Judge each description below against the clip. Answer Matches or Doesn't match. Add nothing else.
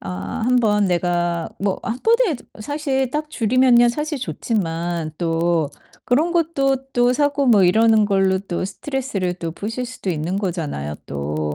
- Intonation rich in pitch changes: Matches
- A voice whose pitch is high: Matches